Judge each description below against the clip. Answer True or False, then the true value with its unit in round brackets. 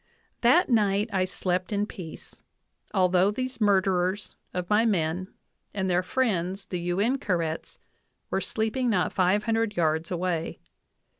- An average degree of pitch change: True (3.3 semitones)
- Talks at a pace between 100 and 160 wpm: True (145 wpm)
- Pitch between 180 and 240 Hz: True (190 Hz)